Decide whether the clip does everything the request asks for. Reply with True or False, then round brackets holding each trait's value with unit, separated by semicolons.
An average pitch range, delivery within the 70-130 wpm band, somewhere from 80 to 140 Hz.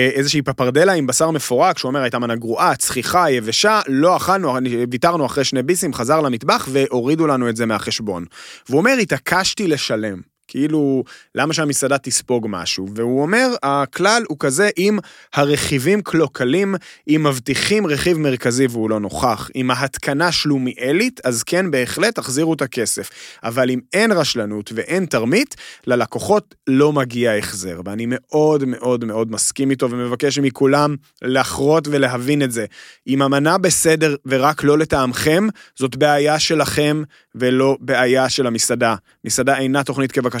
False (3.5 semitones; 145 wpm; 135 Hz)